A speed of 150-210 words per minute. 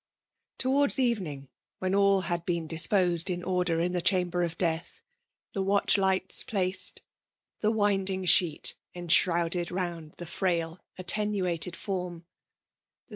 No: slow, 135 wpm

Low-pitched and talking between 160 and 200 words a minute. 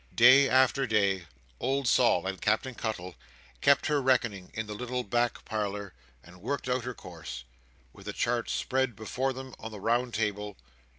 Yes: low, 115 Hz; average, 170 wpm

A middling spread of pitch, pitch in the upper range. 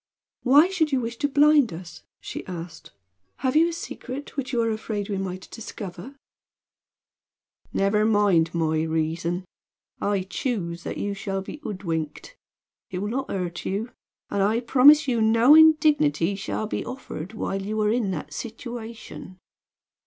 No: wide, 5.9 semitones; high, 215 Hz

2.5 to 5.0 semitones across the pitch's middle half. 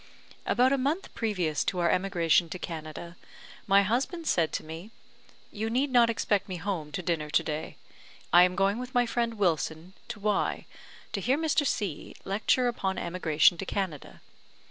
No: wide, 5.6 semitones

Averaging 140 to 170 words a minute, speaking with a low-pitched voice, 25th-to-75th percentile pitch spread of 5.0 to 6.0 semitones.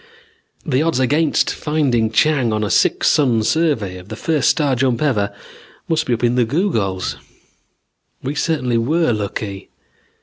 Yes: average, 155 wpm; low, 125 Hz; wide, 5.6 semitones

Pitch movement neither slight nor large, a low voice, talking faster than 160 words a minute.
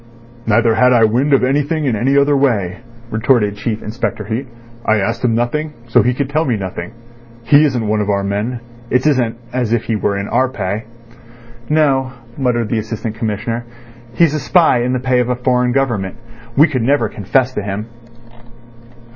Yes: average, 3.5 semitones; low, 120 Hz; average, 190 wpm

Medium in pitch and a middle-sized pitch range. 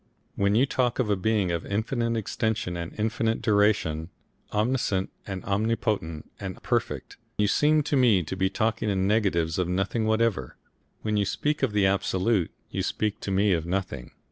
No: low, 105 Hz; average, 3.1 semitones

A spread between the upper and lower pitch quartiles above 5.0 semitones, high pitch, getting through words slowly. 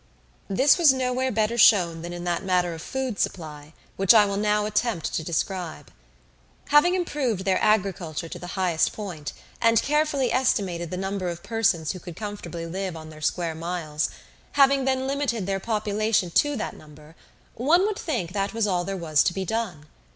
No: wide, 5.5 semitones; high, 195 Hz; average, 180 wpm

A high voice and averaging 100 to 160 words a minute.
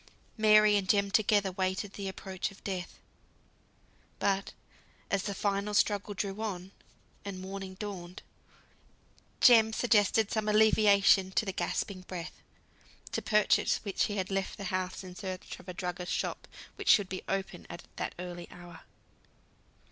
Yes: high, 195 Hz; average, 145 wpm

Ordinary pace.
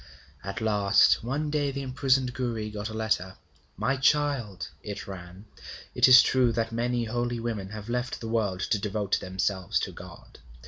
Yes: average, 170 wpm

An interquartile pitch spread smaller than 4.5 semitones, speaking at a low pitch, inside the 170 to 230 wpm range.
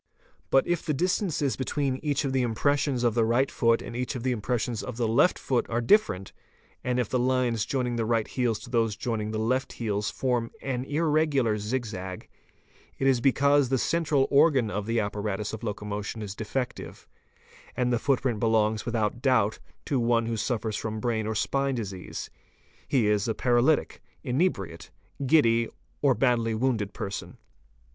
Yes: average, 3.4 semitones; low, 120 Hz; average, 180 wpm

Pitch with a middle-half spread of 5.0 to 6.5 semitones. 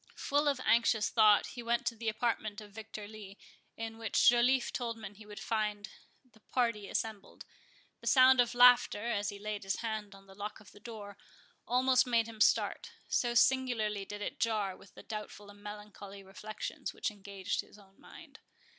No: narrow, 2.5 semitones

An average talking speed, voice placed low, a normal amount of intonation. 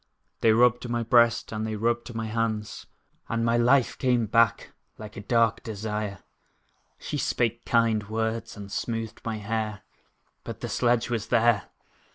No: average, 155 wpm; low, 115 Hz; narrow, 1.5 semitones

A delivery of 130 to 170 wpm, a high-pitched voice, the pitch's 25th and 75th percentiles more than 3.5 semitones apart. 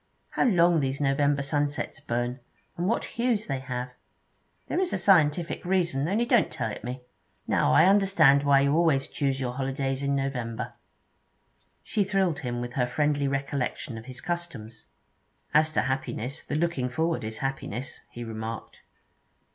No: average, 165 wpm; medium, 140 Hz; average, 4.9 semitones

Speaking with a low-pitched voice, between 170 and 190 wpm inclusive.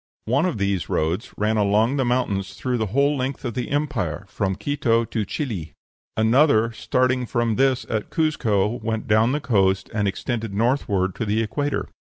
Yes: low, 115 Hz; average, 180 wpm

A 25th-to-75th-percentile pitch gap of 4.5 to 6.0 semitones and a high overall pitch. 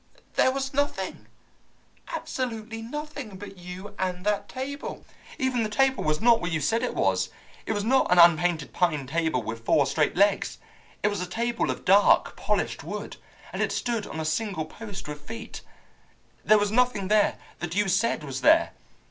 Yes: average, 5.2 semitones; high, 205 Hz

